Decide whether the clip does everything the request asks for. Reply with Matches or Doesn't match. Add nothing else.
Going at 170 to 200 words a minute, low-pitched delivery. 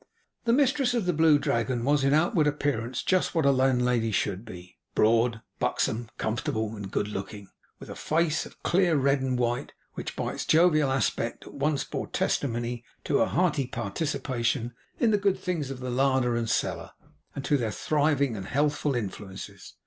Matches